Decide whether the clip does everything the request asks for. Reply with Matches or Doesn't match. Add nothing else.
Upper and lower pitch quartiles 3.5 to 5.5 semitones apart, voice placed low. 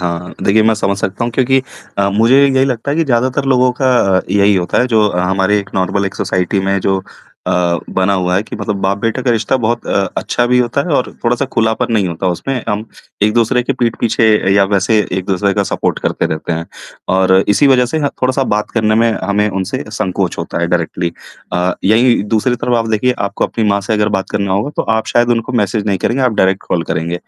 Matches